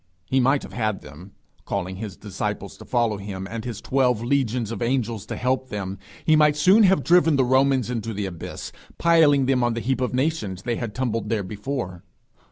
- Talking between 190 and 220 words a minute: Yes, average, 200 wpm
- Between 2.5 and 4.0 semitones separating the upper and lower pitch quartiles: No, average, 4.4 semitones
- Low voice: Yes, low, 120 Hz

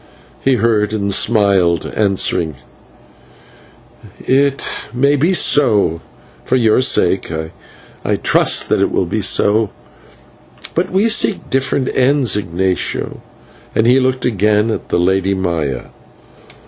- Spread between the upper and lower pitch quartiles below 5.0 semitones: No, average, 5.3 semitones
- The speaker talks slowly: Yes, slow, 120 wpm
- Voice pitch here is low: Yes, low, 110 Hz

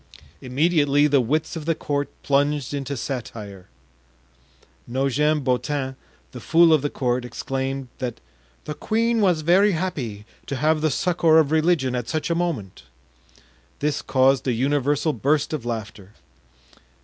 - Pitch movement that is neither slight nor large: Yes, average, 3.6 semitones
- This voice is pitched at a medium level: Yes, medium, 145 Hz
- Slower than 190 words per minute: Yes, average, 140 wpm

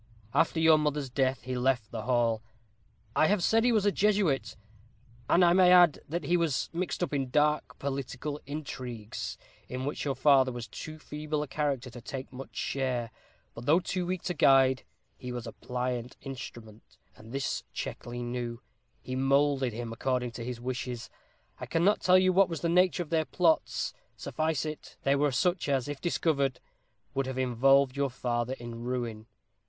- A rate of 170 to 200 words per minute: Yes, average, 180 wpm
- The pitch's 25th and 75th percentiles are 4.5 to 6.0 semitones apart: No, average, 4.1 semitones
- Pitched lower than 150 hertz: Yes, low, 135 Hz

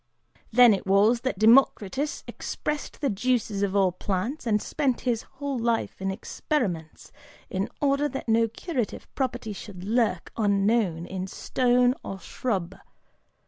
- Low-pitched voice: No, high, 225 Hz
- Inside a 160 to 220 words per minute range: No, average, 140 wpm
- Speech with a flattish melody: No, average, 4.6 semitones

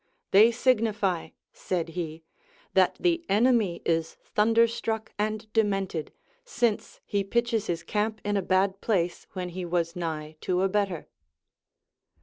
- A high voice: Yes, high, 200 Hz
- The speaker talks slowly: Yes, slow, 130 wpm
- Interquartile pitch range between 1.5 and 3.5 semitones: No, average, 4.1 semitones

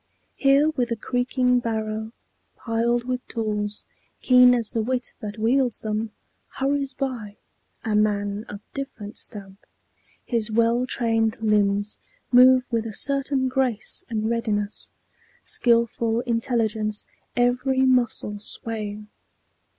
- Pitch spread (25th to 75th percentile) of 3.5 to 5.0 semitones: No, average, 2.8 semitones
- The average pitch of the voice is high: Yes, high, 230 Hz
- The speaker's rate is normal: No, slow, 115 wpm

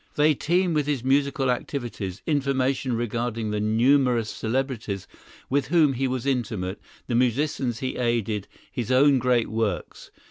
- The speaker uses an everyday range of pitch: Yes, average, 3.3 semitones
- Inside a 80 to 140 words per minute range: Yes, slow, 135 wpm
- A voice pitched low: Yes, low, 125 Hz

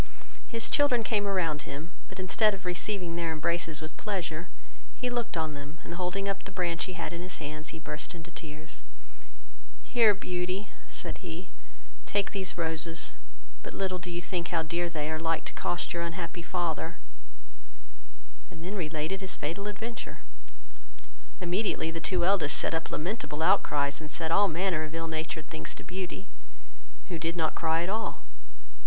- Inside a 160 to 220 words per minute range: Yes, average, 175 wpm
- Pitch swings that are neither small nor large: Yes, average, 3.0 semitones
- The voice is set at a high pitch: No, medium, 175 Hz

